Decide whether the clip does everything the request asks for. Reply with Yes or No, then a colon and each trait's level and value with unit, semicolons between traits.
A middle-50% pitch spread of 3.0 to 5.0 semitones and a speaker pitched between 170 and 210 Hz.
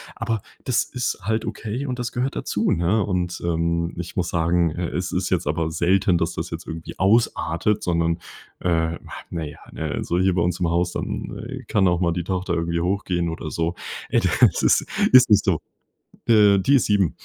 No: average, 3.5 semitones; very low, 90 Hz